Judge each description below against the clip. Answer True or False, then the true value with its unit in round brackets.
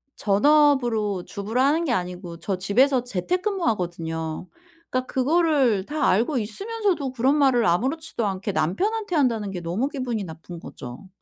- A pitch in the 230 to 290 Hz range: True (235 Hz)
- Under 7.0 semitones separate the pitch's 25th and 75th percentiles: False (7.5 semitones)